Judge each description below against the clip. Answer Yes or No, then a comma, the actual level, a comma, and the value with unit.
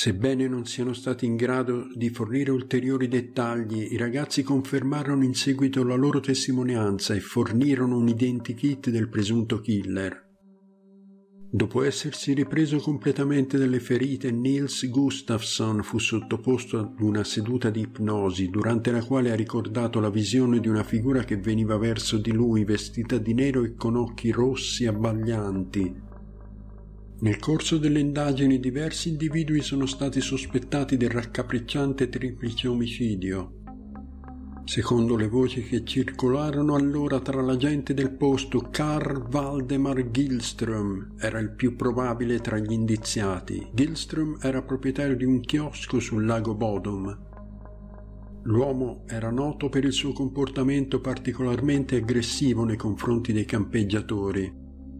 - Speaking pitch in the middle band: No, low, 125 Hz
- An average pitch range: Yes, average, 3.5 semitones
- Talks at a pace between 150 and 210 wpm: No, average, 130 wpm